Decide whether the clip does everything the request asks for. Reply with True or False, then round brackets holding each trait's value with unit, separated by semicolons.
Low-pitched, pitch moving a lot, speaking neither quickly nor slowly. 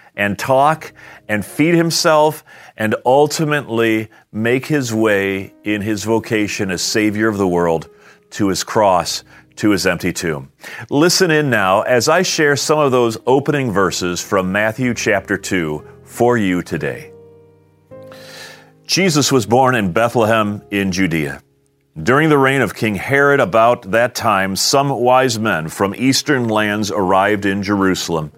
True (110 Hz; 6.1 semitones; 145 wpm)